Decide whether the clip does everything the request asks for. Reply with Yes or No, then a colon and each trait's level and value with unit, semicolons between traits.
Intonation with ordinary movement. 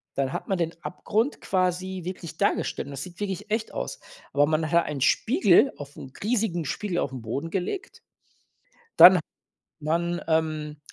Yes: average, 4.3 semitones